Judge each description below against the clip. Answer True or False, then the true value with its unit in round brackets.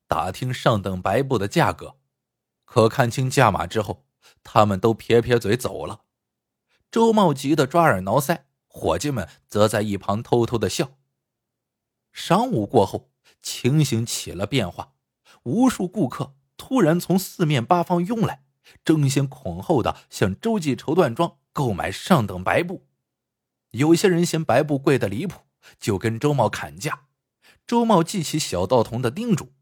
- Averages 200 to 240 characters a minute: True (220 characters per minute)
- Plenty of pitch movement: True (6.5 semitones)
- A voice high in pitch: False (135 Hz)